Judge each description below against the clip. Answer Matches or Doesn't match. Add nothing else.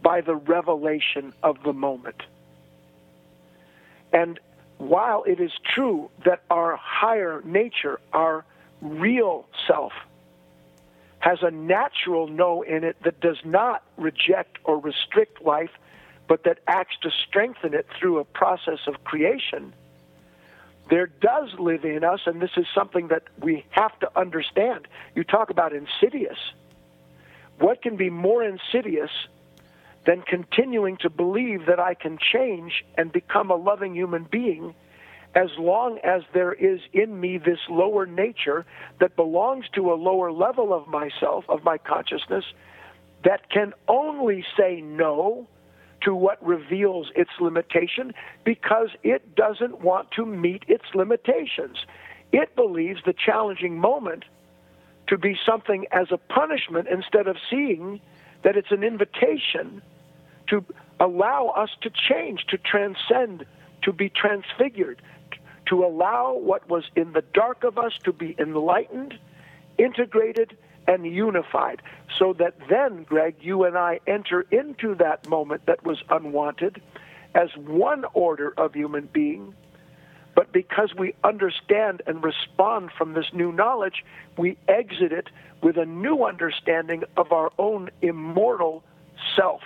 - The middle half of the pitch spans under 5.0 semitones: Matches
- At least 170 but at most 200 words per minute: Doesn't match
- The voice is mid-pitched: Matches